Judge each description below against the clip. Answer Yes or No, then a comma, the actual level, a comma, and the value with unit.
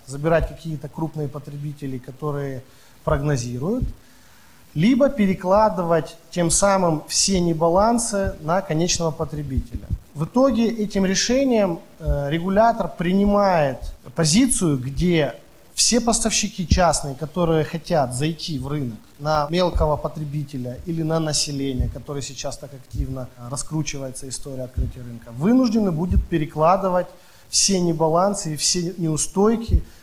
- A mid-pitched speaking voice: Yes, medium, 160 Hz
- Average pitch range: Yes, average, 4.6 semitones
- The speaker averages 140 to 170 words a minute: No, slow, 105 wpm